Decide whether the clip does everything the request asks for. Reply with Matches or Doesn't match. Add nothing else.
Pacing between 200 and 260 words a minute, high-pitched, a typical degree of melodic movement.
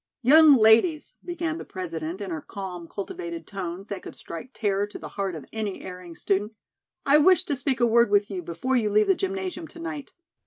Doesn't match